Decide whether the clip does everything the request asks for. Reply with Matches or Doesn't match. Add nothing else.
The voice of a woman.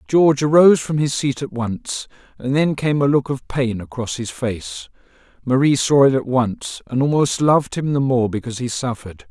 Doesn't match